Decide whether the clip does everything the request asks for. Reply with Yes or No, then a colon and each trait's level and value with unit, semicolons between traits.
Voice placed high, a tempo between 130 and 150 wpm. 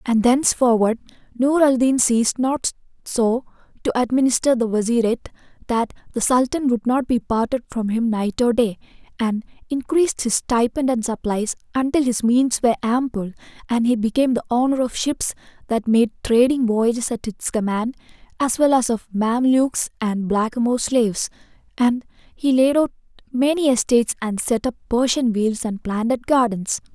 No: high, 240 Hz; average, 160 wpm